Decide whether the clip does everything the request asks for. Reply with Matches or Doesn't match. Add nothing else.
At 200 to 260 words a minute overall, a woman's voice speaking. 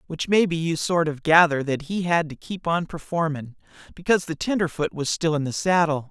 Doesn't match